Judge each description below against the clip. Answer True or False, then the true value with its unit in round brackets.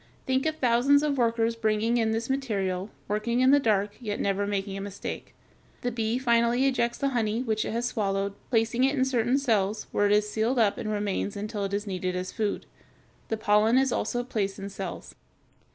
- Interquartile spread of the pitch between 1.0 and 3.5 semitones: True (3.1 semitones)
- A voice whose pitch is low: False (225 Hz)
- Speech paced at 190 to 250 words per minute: True (200 wpm)